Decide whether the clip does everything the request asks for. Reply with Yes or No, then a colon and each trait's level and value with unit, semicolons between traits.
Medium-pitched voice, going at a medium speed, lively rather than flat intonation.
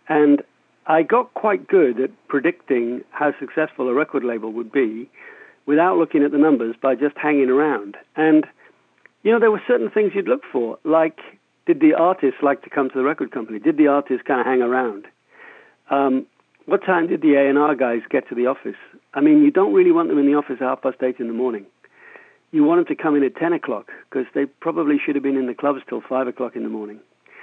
No: medium, 145 Hz; fast, 225 wpm; wide, 7.3 semitones